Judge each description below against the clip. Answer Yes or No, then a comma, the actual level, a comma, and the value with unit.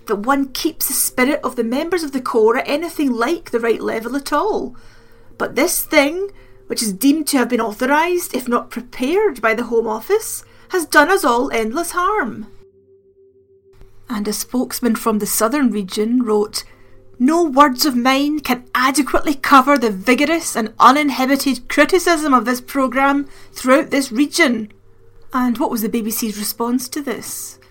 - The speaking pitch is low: No, very high, 265 Hz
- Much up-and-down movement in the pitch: No, average, 4.8 semitones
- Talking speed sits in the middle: Yes, average, 165 wpm